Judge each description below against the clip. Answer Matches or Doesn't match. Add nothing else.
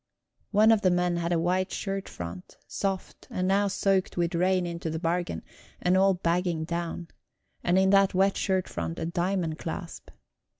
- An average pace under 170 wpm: Doesn't match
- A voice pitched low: Doesn't match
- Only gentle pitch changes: Matches